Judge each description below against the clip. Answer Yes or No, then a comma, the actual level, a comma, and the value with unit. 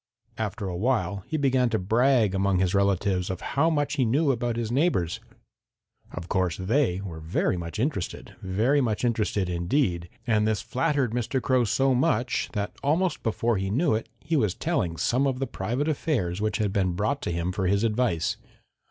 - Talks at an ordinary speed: Yes, average, 185 wpm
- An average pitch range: No, wide, 5.9 semitones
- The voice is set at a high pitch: No, low, 110 Hz